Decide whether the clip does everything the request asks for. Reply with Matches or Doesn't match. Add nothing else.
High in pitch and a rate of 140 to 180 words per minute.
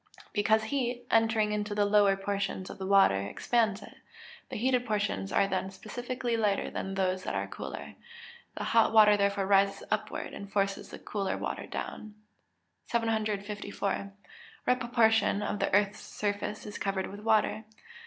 Matches